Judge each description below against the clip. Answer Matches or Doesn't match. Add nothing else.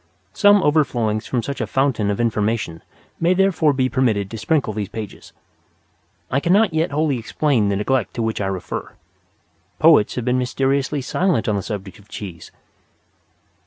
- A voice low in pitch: Matches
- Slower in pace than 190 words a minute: Matches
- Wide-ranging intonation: Matches